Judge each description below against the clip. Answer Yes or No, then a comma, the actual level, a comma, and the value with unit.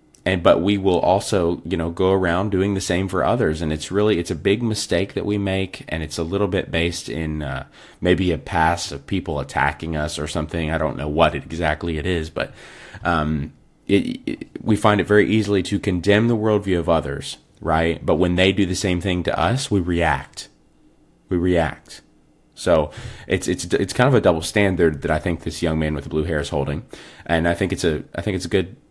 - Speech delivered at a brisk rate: Yes, fast, 225 wpm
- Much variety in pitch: No, average, 3.5 semitones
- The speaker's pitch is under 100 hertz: Yes, very low, 85 Hz